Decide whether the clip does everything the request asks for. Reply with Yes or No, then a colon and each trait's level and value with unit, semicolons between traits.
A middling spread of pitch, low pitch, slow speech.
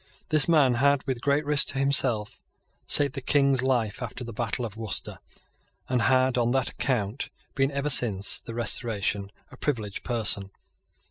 No: average, 3.6 semitones; low, 125 Hz; average, 160 wpm